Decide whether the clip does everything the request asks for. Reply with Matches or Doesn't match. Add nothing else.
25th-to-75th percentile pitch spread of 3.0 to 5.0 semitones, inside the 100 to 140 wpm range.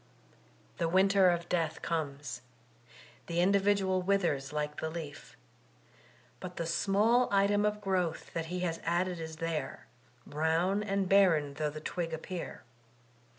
Matches